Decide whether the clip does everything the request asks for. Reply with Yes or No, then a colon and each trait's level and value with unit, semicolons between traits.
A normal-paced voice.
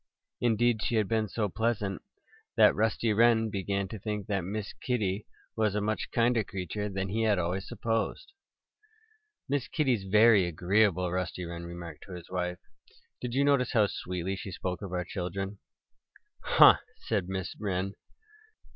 Yes: average, 155 wpm